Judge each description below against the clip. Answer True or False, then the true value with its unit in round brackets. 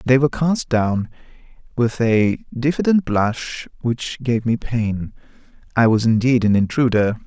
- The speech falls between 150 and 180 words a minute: False (140 wpm)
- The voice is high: False (120 Hz)